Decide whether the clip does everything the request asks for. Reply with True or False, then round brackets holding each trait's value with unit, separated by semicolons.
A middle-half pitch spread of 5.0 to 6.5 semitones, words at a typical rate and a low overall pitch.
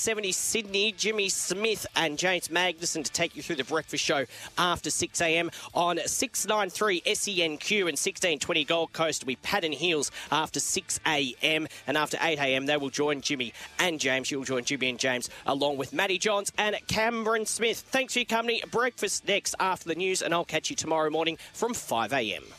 False (5.3 semitones; 180 wpm; 170 Hz)